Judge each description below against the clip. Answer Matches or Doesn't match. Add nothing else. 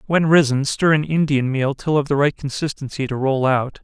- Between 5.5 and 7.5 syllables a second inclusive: Doesn't match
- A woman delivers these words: Doesn't match